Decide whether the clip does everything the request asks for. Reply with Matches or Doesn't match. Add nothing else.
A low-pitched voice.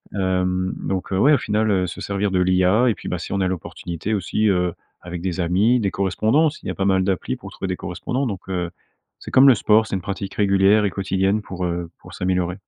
Matches